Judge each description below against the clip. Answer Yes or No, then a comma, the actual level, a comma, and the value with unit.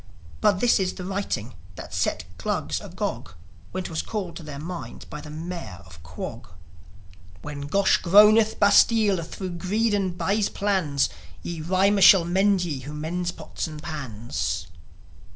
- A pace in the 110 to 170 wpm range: Yes, average, 150 wpm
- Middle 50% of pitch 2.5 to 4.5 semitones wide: No, average, 5.1 semitones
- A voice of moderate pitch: Yes, medium, 175 Hz